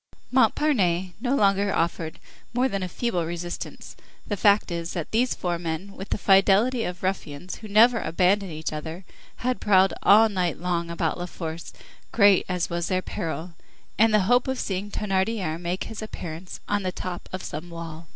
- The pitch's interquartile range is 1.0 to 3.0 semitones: No, average, 3.5 semitones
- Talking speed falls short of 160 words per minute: No, average, 180 wpm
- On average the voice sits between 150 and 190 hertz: Yes, medium, 185 Hz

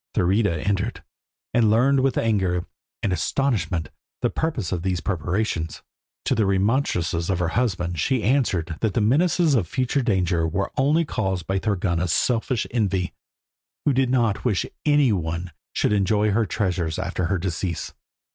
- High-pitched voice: No, low, 100 Hz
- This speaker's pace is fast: No, average, 155 wpm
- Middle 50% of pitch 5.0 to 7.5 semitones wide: Yes, wide, 5.4 semitones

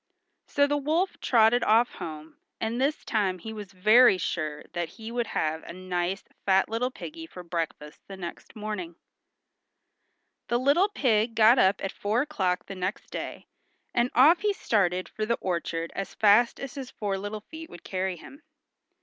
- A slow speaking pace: No, average, 175 wpm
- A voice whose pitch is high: Yes, high, 215 Hz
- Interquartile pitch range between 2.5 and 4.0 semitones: No, average, 5.2 semitones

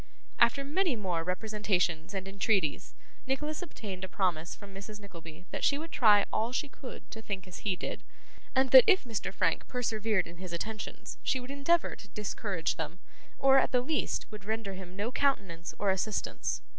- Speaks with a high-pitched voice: Yes, high, 210 Hz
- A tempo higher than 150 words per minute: Yes, average, 180 wpm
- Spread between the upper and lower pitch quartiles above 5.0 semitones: Yes, wide, 5.4 semitones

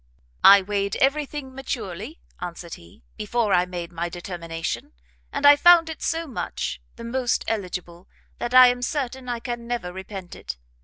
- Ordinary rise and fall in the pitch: No, wide, 6.7 semitones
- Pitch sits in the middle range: No, high, 225 Hz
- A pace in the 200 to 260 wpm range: No, average, 165 wpm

